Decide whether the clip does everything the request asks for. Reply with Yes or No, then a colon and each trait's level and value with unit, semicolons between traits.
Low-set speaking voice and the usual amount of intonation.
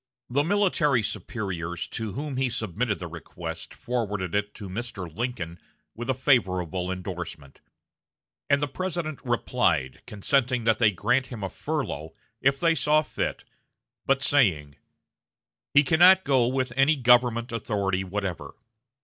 No: low, 120 Hz; wide, 6.3 semitones